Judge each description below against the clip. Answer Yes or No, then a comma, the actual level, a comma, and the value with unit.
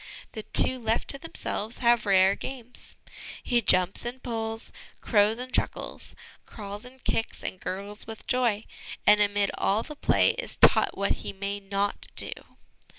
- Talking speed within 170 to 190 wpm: No, average, 155 wpm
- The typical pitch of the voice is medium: No, high, 220 Hz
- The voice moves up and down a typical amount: Yes, average, 3.1 semitones